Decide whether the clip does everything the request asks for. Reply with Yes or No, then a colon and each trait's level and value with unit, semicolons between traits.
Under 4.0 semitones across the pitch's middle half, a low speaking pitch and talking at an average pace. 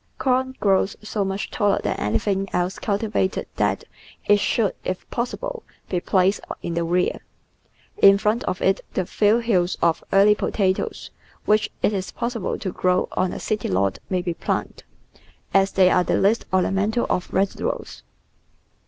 No: narrow, 2.6 semitones; high, 195 Hz; average, 160 wpm